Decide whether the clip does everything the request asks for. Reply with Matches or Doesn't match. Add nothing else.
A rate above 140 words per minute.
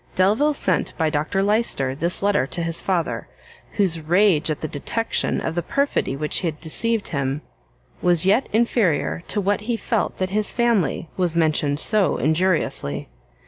Matches